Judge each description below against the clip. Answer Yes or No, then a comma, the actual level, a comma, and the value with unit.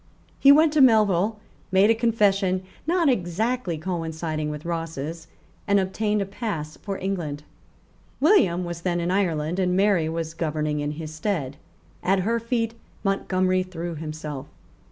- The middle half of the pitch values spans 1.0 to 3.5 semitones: No, average, 4.5 semitones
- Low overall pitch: No, medium, 185 Hz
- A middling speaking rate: Yes, average, 145 wpm